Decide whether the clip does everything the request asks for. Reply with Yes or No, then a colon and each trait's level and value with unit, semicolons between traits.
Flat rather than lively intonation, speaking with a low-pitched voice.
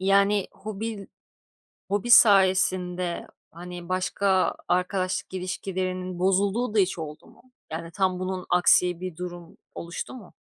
No: narrow, 1.6 semitones; medium, 185 Hz